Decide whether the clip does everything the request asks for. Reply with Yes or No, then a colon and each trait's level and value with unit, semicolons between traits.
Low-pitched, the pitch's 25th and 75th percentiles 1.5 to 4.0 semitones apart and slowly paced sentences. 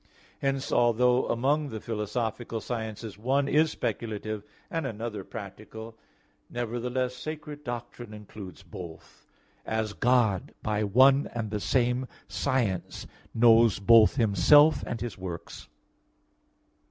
Yes: low, 115 Hz; average, 3.1 semitones; slow, 110 wpm